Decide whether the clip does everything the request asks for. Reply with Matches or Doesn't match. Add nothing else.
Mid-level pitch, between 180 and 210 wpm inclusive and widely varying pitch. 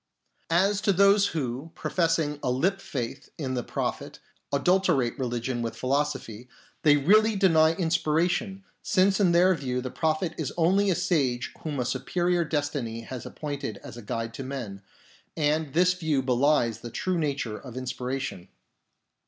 Doesn't match